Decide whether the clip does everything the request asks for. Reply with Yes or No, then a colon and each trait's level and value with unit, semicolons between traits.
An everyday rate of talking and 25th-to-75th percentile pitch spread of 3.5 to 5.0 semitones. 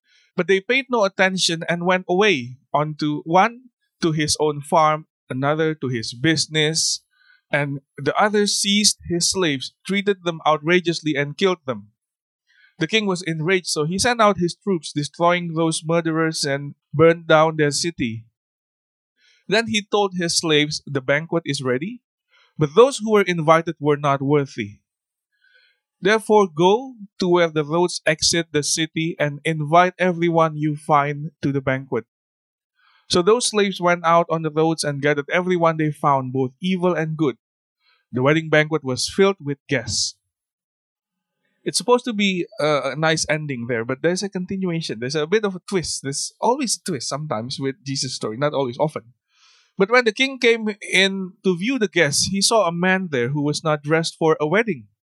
Yes: average, 170 wpm; average, 4.6 semitones